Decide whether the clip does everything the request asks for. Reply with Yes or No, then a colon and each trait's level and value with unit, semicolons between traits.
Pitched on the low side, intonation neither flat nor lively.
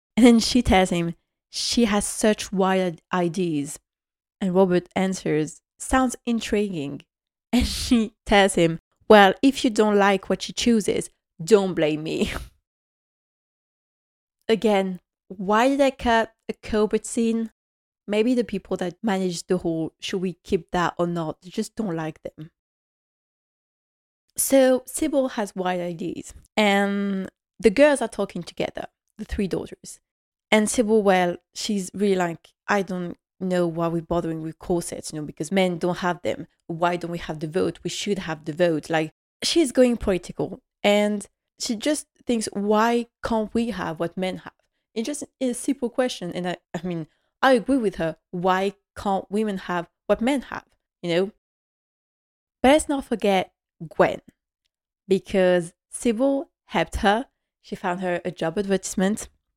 No: high, 195 Hz; average, 4.5 semitones